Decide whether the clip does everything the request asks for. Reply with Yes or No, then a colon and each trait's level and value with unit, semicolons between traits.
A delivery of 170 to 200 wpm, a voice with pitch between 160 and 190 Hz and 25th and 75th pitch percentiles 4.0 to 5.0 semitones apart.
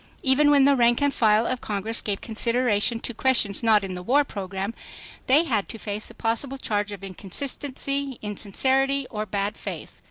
No: average, 180 wpm; high, 230 Hz; average, 4.6 semitones